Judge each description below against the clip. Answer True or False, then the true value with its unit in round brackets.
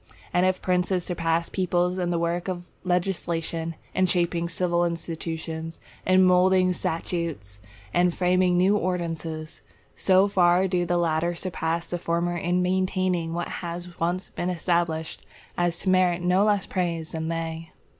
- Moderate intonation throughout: False (1.5 semitones)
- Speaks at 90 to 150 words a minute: True (145 wpm)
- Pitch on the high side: False (175 Hz)